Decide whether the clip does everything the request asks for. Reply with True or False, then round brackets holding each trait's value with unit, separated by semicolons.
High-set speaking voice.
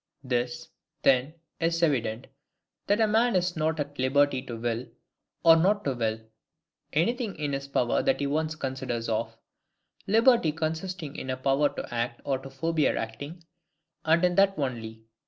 False (145 Hz)